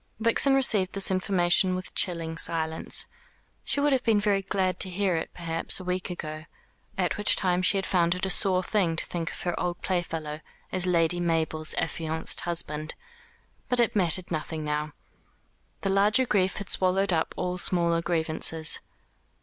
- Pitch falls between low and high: Yes, medium, 180 Hz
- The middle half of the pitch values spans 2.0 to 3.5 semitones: Yes, average, 2.9 semitones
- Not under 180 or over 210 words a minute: No, average, 170 wpm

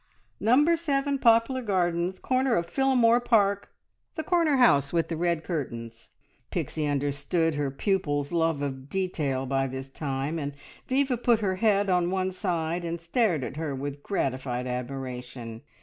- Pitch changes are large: Yes, wide, 8.1 semitones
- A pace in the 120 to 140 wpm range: No, average, 150 wpm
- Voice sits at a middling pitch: Yes, medium, 170 Hz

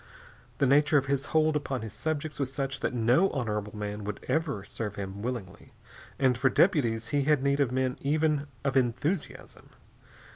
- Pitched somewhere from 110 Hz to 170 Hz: Yes, low, 135 Hz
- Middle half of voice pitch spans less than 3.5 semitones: No, average, 4.4 semitones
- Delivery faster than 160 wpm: Yes, average, 175 wpm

